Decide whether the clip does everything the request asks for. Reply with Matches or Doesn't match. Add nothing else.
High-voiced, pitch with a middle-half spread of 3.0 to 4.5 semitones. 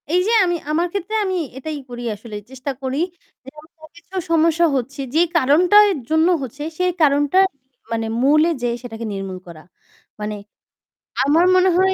Doesn't match